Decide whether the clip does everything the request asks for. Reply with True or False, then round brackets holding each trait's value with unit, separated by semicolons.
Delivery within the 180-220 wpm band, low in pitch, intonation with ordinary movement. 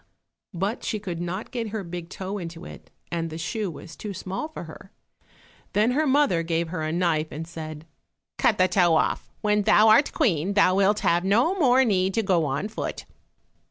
False (195 wpm; 185 Hz; 4.2 semitones)